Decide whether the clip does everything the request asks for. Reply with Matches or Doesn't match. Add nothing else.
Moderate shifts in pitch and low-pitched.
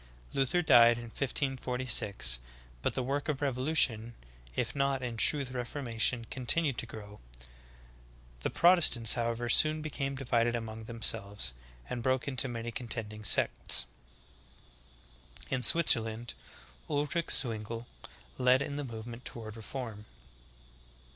Matches